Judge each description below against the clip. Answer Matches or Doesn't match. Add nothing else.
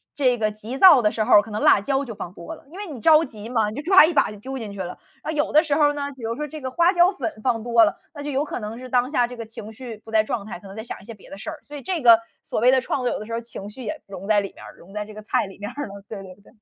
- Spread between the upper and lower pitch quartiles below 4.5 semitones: Doesn't match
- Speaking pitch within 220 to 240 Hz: Matches